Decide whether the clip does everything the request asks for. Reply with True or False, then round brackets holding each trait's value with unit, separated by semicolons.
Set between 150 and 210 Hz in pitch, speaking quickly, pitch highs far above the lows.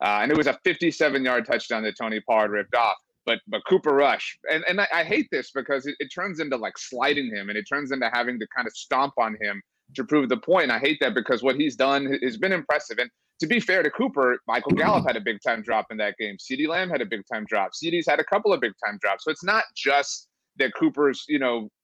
False (140 Hz; 260 wpm; 5.7 semitones)